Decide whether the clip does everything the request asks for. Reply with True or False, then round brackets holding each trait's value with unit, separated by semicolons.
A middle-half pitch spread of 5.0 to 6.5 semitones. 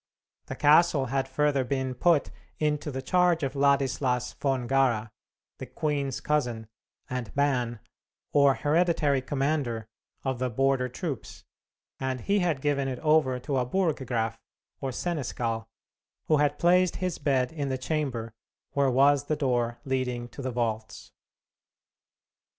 False (2.9 semitones)